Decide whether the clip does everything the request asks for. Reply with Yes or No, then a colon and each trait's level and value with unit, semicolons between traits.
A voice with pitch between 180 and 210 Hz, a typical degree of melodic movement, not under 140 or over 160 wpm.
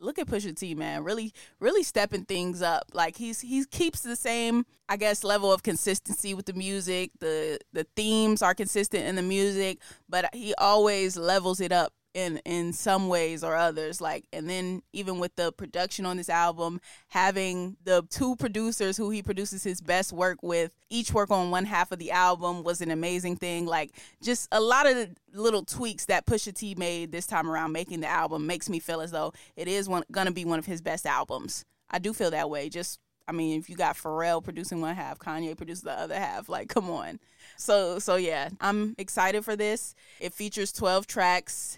No: medium, 185 Hz; average, 3.4 semitones; fast, 205 wpm